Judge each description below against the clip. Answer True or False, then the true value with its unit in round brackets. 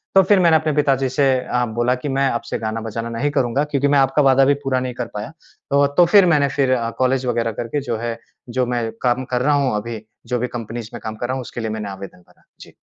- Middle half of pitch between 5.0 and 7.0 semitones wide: False (3.2 semitones)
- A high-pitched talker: False (125 Hz)